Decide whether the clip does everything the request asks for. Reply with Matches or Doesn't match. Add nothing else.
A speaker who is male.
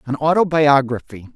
Matches